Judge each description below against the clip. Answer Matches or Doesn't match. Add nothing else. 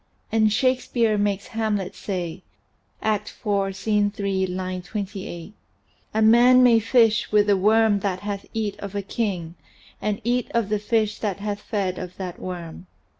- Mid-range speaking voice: Doesn't match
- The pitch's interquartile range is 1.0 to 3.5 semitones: Matches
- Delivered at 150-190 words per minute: Matches